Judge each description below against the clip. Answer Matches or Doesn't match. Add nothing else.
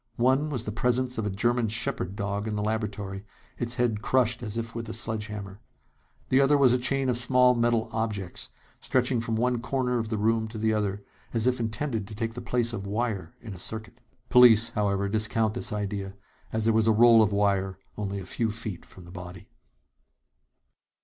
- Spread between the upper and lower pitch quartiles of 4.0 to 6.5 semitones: Doesn't match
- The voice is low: Matches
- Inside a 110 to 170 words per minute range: Doesn't match